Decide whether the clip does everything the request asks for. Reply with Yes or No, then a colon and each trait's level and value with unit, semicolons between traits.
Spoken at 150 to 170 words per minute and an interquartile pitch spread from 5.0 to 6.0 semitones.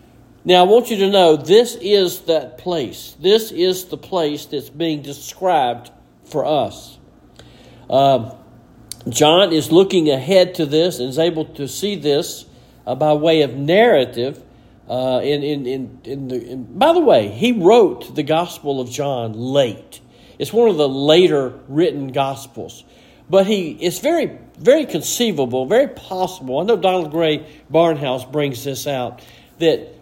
Yes: average, 155 wpm; wide, 5.5 semitones